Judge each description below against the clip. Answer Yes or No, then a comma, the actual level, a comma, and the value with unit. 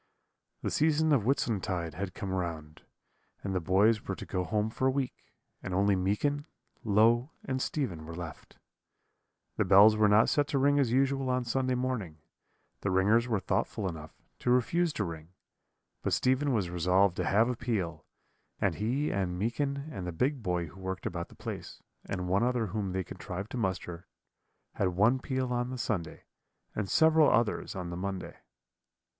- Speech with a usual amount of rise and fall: No, wide, 5.7 semitones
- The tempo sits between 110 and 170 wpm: No, average, 180 wpm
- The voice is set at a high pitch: No, low, 105 Hz